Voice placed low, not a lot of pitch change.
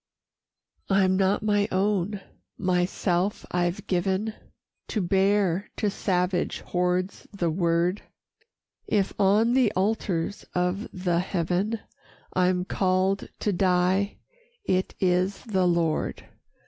No: medium, 185 Hz; narrow, 2.1 semitones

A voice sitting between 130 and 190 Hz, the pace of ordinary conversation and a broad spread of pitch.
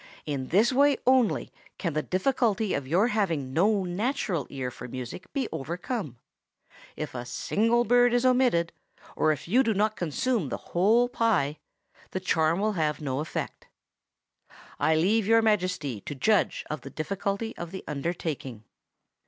Yes: medium, 185 Hz; average, 155 wpm; wide, 6.8 semitones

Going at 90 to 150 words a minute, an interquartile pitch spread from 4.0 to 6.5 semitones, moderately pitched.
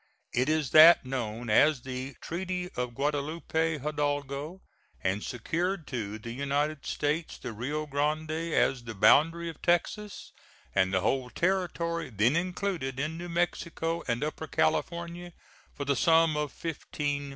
Yes: average, 140 wpm; average, 4.3 semitones; medium, 150 Hz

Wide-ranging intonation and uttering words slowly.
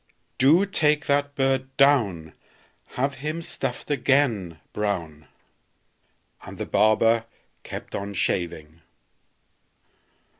Yes: wide, 6.6 semitones; slow, 90 wpm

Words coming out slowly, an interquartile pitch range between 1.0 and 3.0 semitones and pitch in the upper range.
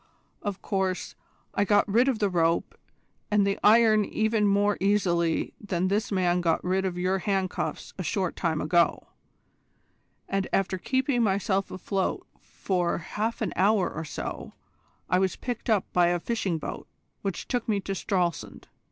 No: average, 160 wpm; average, 2.7 semitones; high, 195 Hz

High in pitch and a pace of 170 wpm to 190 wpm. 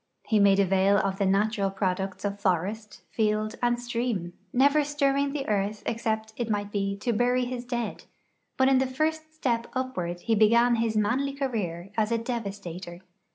Yes: high, 220 Hz; average, 175 wpm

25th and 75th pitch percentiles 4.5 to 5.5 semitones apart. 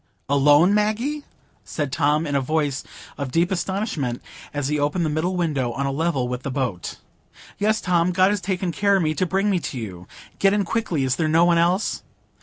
Yes: average, 5.2 semitones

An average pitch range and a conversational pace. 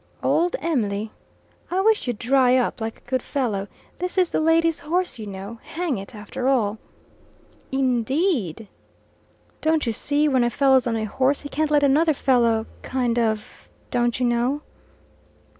Yes: average, 4.9 semitones; average, 170 wpm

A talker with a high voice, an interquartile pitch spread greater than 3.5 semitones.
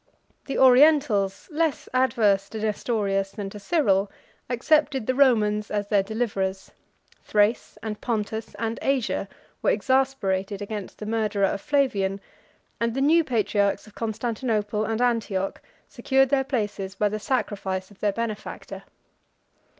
Yes: high, 215 Hz; average, 4.2 semitones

